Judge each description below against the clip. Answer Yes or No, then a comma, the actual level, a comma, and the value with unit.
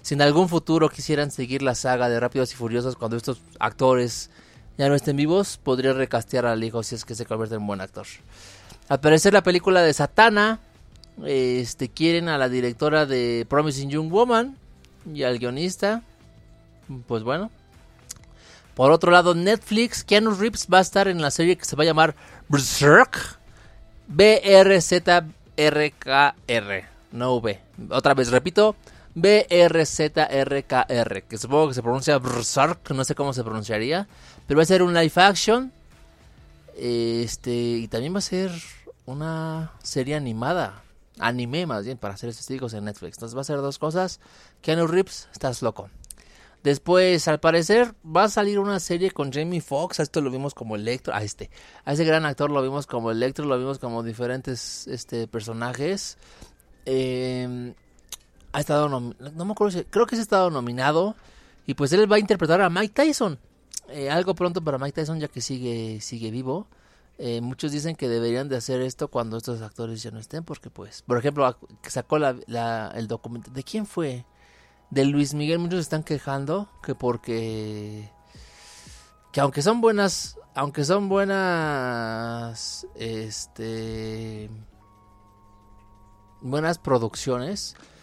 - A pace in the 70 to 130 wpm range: No, average, 160 wpm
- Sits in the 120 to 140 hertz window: Yes, low, 135 Hz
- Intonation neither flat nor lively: No, wide, 6.0 semitones